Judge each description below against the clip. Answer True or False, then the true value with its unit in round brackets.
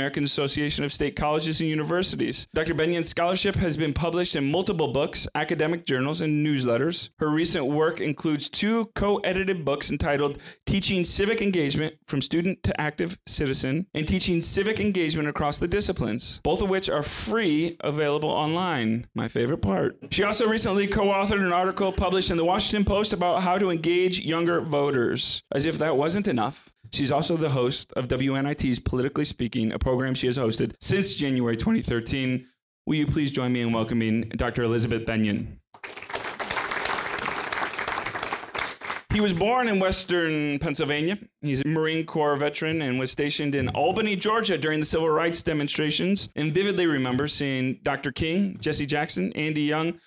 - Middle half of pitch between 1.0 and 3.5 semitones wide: False (4.4 semitones)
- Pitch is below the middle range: False (155 Hz)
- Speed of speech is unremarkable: True (160 wpm)